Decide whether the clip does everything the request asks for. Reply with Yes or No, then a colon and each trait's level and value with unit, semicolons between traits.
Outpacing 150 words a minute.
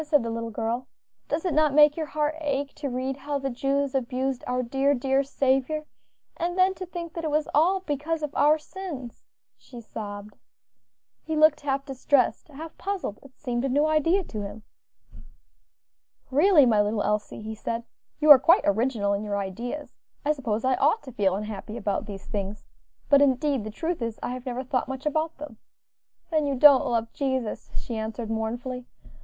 Yes: average, 185 wpm